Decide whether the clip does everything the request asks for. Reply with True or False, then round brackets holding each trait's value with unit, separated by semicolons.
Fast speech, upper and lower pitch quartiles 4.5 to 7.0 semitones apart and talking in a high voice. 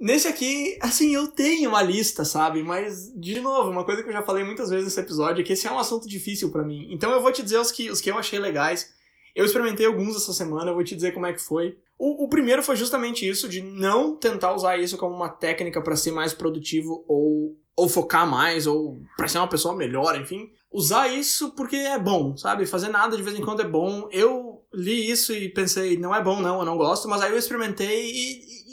True (240 wpm; 5.3 semitones; 195 Hz)